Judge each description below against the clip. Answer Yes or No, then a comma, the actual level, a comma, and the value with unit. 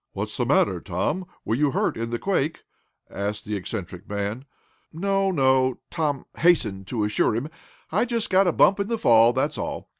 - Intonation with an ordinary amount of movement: No, wide, 8.9 semitones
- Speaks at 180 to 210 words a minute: Yes, average, 185 wpm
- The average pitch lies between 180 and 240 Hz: No, low, 130 Hz